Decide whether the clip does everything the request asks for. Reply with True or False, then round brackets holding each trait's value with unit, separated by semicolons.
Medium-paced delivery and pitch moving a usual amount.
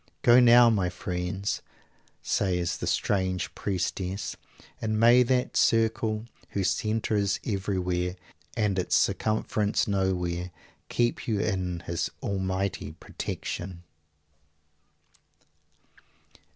False (95 wpm; 3.2 semitones)